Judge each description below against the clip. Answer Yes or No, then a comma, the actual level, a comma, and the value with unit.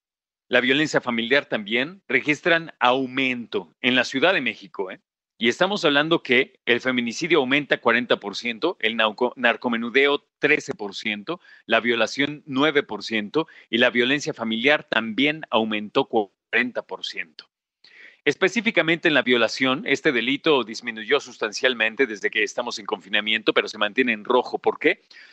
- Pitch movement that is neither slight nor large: Yes, average, 4.0 semitones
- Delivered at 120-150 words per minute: Yes, slow, 125 wpm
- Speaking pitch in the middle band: No, low, 125 Hz